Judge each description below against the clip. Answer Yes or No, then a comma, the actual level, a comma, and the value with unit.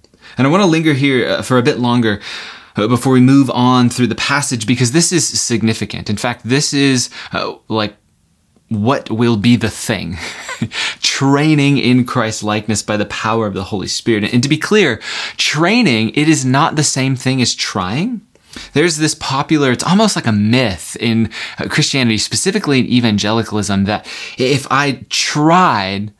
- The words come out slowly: No, average, 165 wpm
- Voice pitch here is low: Yes, low, 125 Hz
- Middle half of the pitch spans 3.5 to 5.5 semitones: Yes, average, 4.4 semitones